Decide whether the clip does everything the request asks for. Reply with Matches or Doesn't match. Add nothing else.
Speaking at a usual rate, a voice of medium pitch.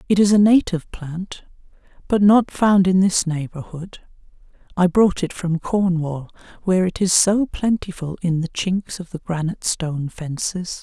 Matches